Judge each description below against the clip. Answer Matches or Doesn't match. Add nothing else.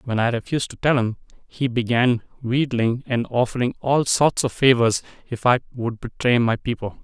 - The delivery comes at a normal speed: Matches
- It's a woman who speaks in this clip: Doesn't match